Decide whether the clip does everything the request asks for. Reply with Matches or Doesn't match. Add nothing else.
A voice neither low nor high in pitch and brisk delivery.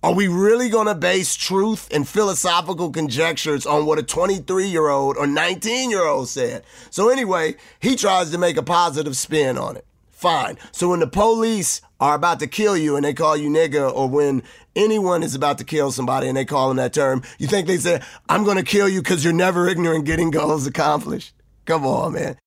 Matches